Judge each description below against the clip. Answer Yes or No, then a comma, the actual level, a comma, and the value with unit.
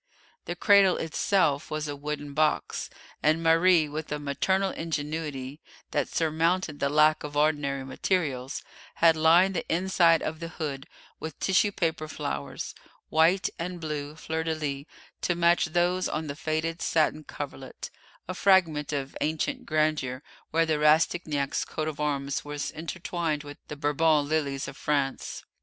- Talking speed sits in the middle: Yes, average, 150 wpm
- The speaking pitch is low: No, medium, 155 Hz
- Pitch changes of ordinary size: No, narrow, 2.2 semitones